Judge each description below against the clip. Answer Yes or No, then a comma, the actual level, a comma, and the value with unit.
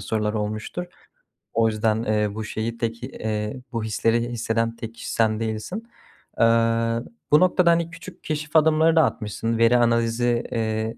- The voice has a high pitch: No, low, 115 Hz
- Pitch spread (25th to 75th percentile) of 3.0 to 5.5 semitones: No, narrow, 2.4 semitones